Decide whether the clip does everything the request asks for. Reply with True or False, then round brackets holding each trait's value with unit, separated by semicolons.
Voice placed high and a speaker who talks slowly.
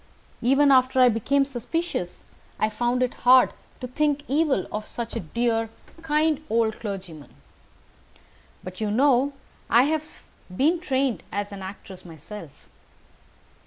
True (245 Hz; 130 wpm)